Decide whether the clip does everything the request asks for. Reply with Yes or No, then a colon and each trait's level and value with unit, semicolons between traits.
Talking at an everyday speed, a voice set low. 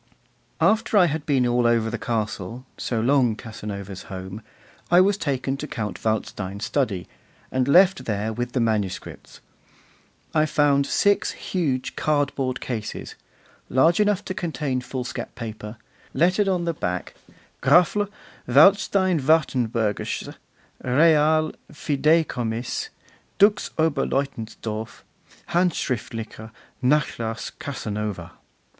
No: slow, 105 wpm; low, 130 Hz